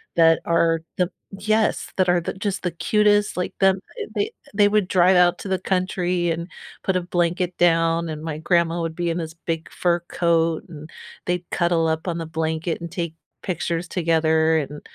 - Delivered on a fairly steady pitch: Yes, narrow, 1.8 semitones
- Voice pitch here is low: No, medium, 170 Hz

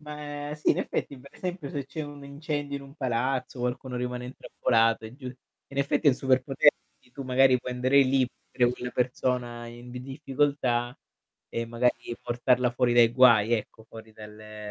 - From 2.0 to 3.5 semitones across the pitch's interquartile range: Yes, narrow, 2.6 semitones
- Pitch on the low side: Yes, low, 125 Hz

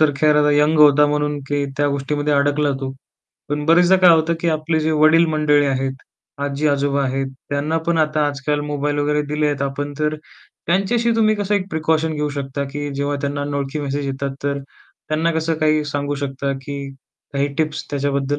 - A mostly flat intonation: Yes, narrow, 1.6 semitones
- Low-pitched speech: No, medium, 145 Hz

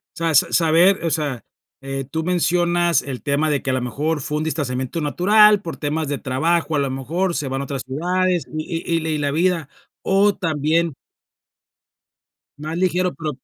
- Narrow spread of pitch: No, average, 3.5 semitones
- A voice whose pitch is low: No, medium, 160 Hz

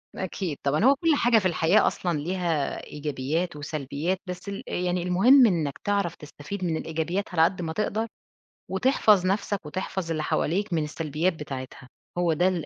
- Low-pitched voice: No, medium, 175 Hz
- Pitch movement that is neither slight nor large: Yes, average, 4.0 semitones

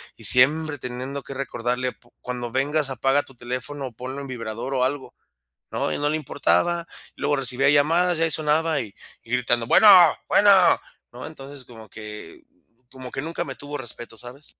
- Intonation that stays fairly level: No, average, 3.1 semitones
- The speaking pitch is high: No, low, 135 Hz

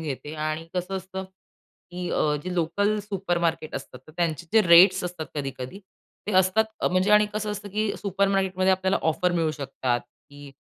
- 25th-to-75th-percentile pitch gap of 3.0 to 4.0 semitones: Yes, average, 3.5 semitones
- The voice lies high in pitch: No, medium, 180 Hz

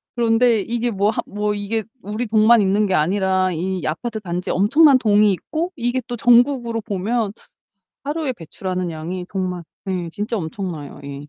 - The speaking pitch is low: No, high, 205 Hz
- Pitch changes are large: No, average, 4.3 semitones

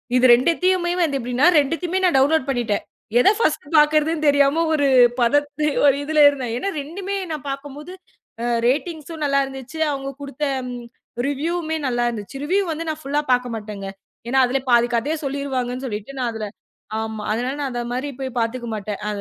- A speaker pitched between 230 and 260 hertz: No, very high, 275 Hz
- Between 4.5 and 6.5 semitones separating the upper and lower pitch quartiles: No, average, 4.0 semitones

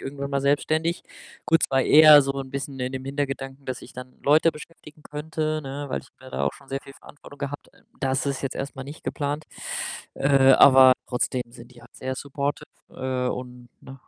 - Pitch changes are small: Yes, narrow, 1.7 semitones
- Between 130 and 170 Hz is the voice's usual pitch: Yes, low, 135 Hz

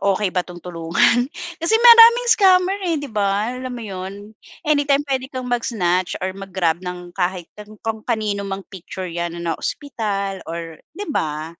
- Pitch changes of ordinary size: No, wide, 6.3 semitones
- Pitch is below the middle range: No, high, 200 Hz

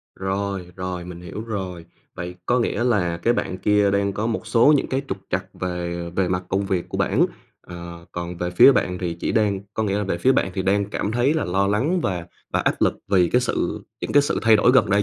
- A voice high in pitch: No, very low, 95 Hz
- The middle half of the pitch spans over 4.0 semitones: No, average, 3.7 semitones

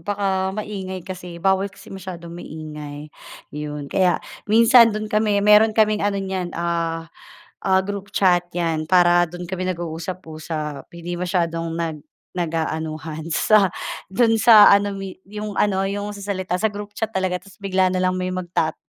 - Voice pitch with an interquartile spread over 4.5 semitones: No, average, 3.2 semitones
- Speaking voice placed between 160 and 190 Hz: Yes, medium, 185 Hz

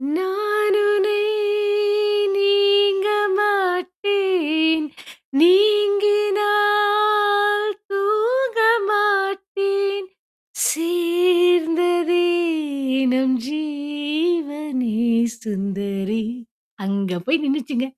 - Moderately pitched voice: No, very high, 375 Hz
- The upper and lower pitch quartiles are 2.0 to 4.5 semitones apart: No, average, 5.1 semitones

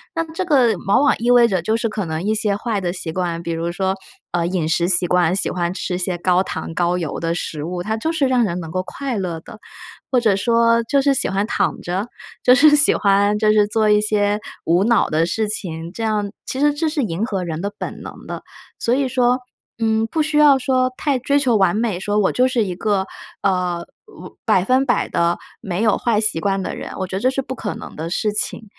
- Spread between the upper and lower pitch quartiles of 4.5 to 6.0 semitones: Yes, average, 5.2 semitones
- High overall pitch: Yes, high, 210 Hz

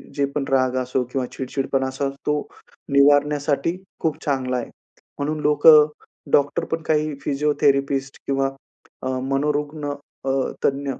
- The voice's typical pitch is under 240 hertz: Yes, medium, 140 Hz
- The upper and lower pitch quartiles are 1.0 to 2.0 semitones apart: Yes, narrow, 1.5 semitones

